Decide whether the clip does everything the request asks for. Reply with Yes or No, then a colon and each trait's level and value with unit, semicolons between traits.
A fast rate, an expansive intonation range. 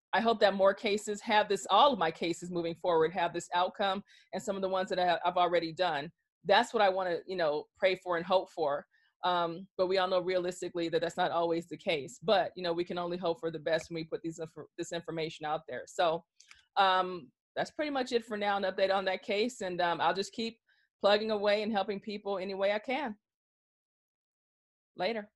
No: fast, 225 wpm; average, 3.1 semitones